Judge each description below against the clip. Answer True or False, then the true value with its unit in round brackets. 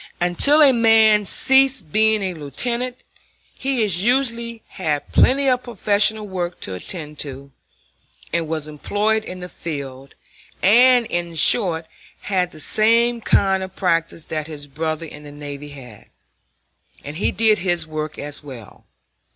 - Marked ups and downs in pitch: True (6.6 semitones)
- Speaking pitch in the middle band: True (180 Hz)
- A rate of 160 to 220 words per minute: False (145 wpm)